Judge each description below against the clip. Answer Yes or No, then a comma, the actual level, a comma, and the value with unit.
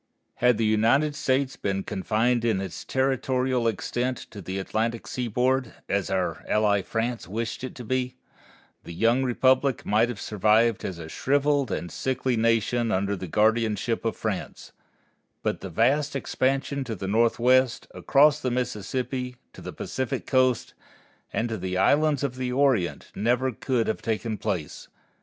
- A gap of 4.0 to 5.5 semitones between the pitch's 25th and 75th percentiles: No, average, 3.3 semitones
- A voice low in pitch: Yes, low, 120 Hz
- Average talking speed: Yes, average, 155 wpm